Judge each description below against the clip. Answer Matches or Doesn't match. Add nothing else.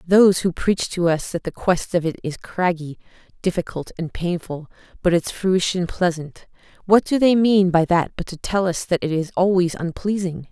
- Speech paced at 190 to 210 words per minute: Matches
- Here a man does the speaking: Doesn't match